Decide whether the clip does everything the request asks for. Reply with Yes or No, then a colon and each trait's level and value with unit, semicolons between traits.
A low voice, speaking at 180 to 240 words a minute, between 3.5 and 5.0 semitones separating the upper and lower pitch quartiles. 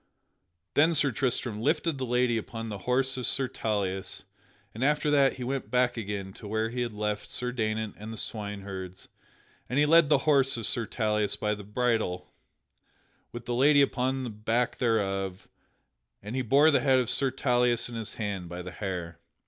Yes: low, 115 Hz; average, 190 wpm; average, 3.9 semitones